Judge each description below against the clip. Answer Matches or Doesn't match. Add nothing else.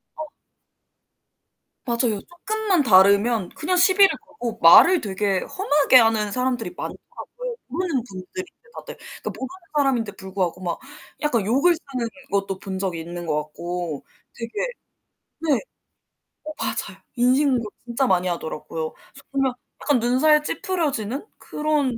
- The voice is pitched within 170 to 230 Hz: Doesn't match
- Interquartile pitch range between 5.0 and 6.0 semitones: Doesn't match